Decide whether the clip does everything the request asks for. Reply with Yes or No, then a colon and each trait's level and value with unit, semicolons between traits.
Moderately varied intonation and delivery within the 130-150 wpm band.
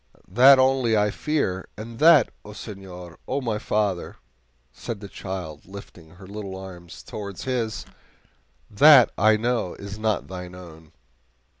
Yes: average, 4.1 semitones; average, 140 wpm